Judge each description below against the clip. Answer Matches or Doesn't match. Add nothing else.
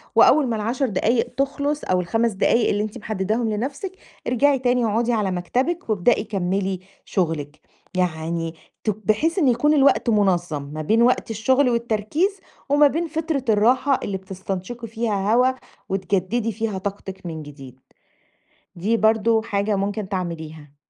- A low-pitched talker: Doesn't match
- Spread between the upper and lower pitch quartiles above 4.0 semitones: Matches